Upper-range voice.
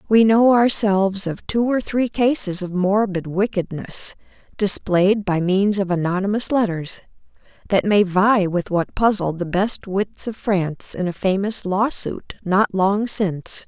Yes: high, 195 Hz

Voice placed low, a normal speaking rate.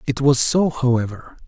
Yes: low, 130 Hz; average, 165 wpm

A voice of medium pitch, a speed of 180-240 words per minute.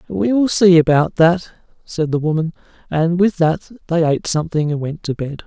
Yes: medium, 165 Hz; average, 200 wpm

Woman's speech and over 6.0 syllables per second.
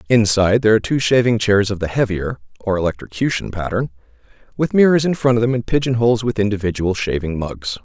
No: male; 6.4 syllables/s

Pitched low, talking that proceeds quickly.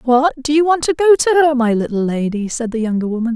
No: very high, 260 Hz; fast, 270 wpm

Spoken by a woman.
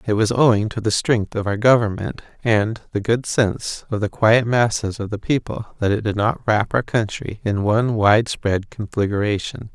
No: male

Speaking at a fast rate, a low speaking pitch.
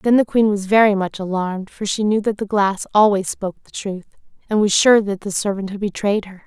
No: fast, 240 wpm; high, 200 Hz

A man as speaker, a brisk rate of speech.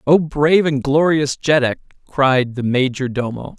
No: male; average, 150 wpm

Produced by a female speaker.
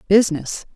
Yes: female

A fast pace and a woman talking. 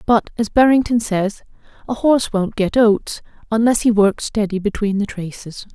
No: average, 165 wpm; female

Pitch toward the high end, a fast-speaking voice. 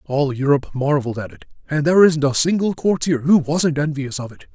No: medium, 145 Hz; fast, 210 wpm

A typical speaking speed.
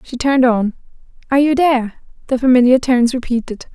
Yes: average, 160 wpm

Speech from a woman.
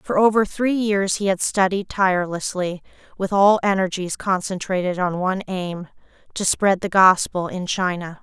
Yes: female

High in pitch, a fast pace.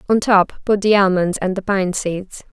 Yes: high, 195 Hz; fast, 210 wpm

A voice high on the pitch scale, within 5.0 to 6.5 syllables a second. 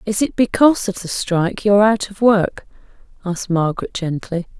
Yes: high, 200 Hz; 5.5 syllables/s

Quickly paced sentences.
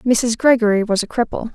No: average, 195 wpm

